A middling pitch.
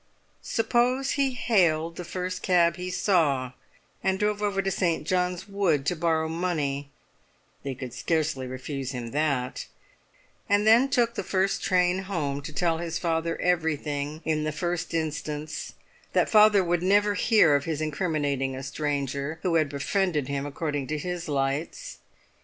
Yes: medium, 165 Hz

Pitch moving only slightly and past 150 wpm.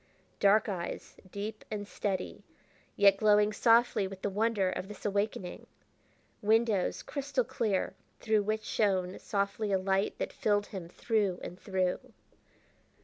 No: narrow, 2.1 semitones; slow, 135 wpm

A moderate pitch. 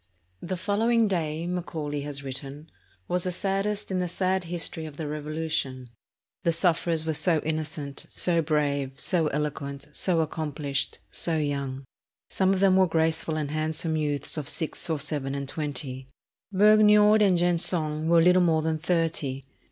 Yes: medium, 160 Hz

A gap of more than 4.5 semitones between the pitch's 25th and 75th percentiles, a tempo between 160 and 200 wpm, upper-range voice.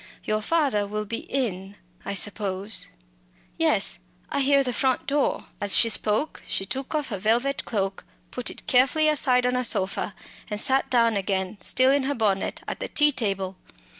Yes: average, 4.9 semitones; average, 175 wpm; high, 230 Hz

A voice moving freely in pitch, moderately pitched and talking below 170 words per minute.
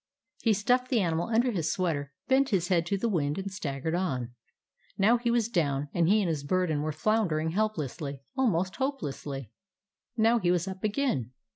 No: wide, 6.3 semitones; medium, 180 Hz; average, 180 wpm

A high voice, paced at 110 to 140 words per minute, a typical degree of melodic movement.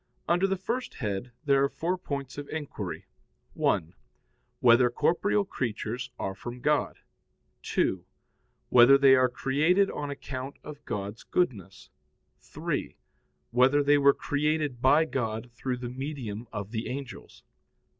No: low, 135 Hz; slow, 135 wpm; average, 3.8 semitones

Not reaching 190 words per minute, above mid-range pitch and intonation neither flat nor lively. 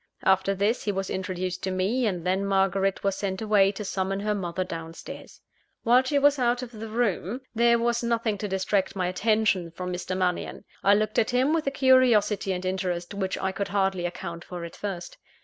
No: fast, 205 wpm; high, 195 Hz; average, 3.2 semitones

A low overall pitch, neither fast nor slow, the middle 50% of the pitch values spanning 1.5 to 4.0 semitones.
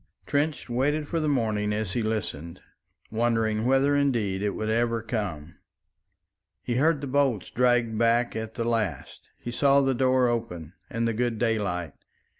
Yes: low, 115 Hz; average, 160 wpm; average, 3.3 semitones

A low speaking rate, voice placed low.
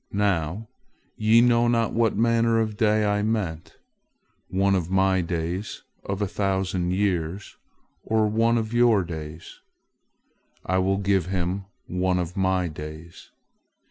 Yes: slow, 130 wpm; very low, 95 Hz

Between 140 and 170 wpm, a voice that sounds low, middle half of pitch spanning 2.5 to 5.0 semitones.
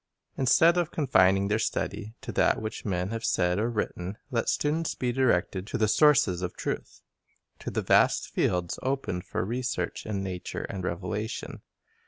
No: average, 165 wpm; low, 110 Hz; wide, 5.5 semitones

